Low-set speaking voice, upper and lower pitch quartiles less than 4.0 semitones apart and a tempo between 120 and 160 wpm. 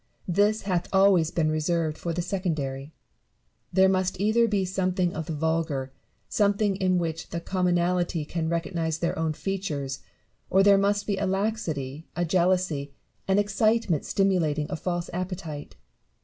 No: medium, 175 Hz; average, 3.3 semitones; average, 150 wpm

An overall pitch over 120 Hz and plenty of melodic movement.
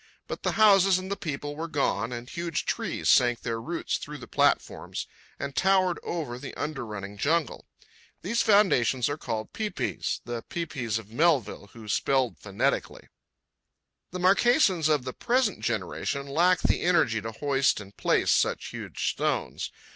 Yes: medium, 140 Hz; wide, 6.9 semitones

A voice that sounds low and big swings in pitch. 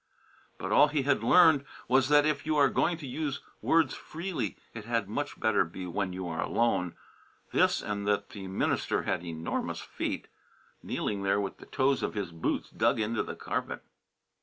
Yes: low, 115 Hz; wide, 6.7 semitones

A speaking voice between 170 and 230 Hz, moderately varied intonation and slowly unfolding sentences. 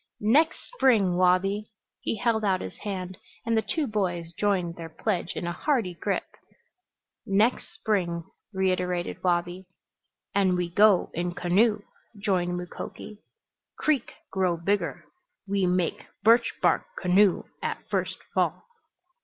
Yes: high, 190 Hz; average, 3.1 semitones; slow, 130 wpm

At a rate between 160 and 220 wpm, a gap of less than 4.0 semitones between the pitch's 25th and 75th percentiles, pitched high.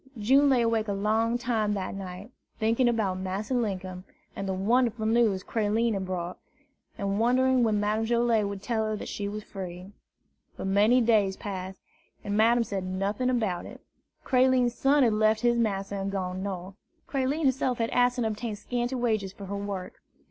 Yes: average, 180 wpm; average, 3.4 semitones; high, 215 Hz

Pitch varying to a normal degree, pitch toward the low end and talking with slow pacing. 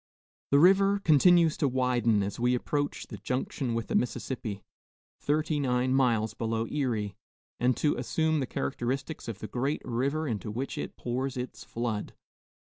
No: average, 4.0 semitones; low, 125 Hz; average, 155 wpm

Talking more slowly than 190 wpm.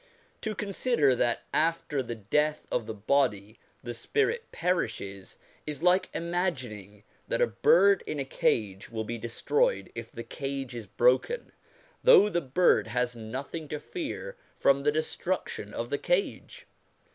Yes: average, 145 wpm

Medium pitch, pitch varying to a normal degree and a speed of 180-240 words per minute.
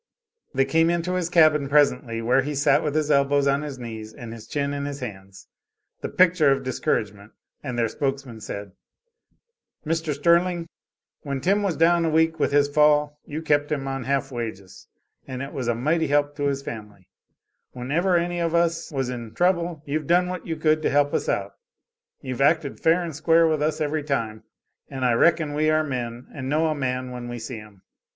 Yes: medium, 145 Hz; average, 4.0 semitones; average, 200 wpm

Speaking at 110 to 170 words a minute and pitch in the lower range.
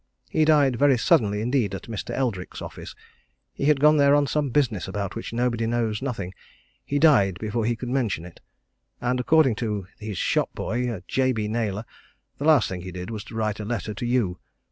No: average, 195 wpm; low, 115 Hz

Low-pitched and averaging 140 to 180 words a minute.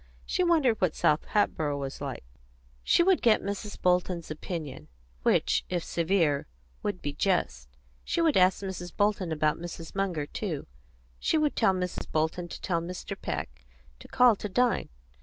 No: medium, 180 Hz; average, 160 wpm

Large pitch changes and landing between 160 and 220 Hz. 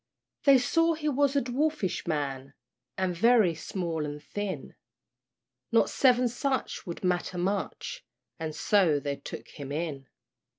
Yes: wide, 8.7 semitones; medium, 185 Hz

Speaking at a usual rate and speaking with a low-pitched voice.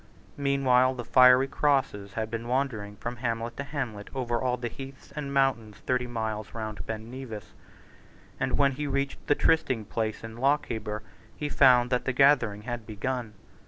Yes: average, 165 wpm; low, 125 Hz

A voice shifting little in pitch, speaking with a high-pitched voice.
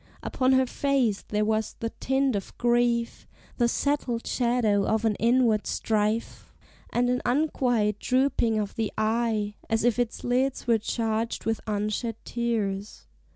Yes: narrow, 2.3 semitones; high, 230 Hz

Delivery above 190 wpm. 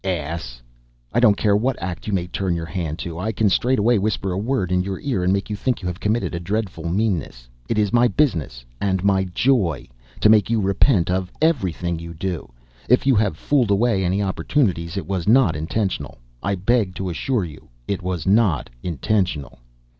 Yes: average, 200 wpm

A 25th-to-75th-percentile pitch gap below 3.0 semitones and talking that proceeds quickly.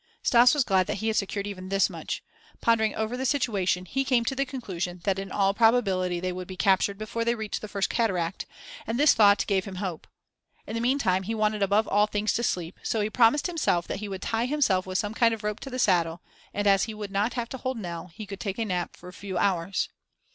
No: average, 3.5 semitones; fast, 250 wpm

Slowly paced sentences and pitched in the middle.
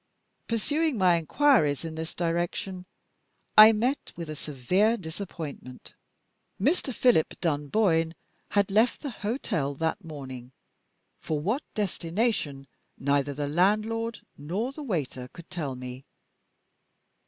Yes: slow, 115 wpm; medium, 170 Hz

